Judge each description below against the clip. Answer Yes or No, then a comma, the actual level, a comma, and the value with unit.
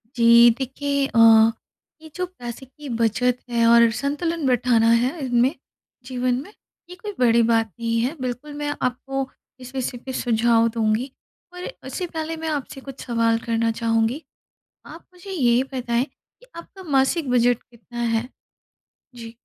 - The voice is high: Yes, very high, 250 Hz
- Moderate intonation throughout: Yes, average, 3.5 semitones